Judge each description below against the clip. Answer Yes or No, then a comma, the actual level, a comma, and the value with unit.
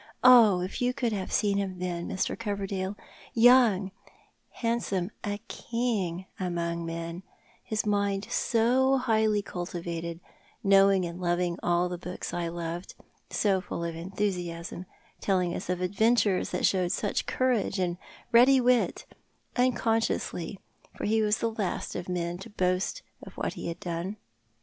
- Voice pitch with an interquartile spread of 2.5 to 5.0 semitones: Yes, average, 3.9 semitones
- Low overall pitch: No, high, 190 Hz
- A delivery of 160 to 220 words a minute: No, average, 150 wpm